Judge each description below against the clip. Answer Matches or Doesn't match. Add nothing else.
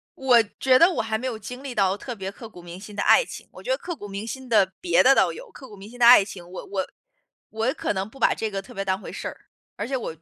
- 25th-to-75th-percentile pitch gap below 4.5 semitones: Doesn't match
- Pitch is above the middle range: Matches